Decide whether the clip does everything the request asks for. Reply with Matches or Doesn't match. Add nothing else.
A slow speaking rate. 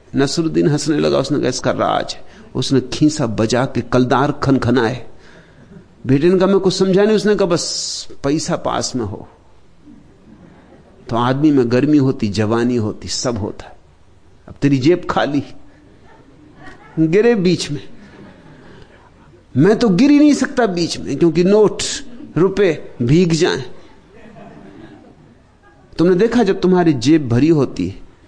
Doesn't match